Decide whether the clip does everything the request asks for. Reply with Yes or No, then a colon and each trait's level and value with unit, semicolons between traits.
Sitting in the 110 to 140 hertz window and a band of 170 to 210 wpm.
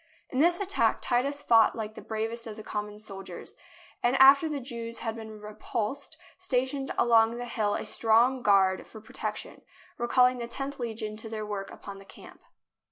No: high, 230 Hz; average, 180 wpm